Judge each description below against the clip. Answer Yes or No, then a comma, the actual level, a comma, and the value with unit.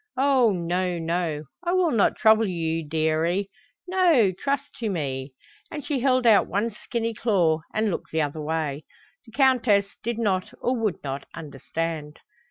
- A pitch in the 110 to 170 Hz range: No, high, 195 Hz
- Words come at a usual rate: Yes, average, 160 wpm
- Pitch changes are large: Yes, wide, 6.6 semitones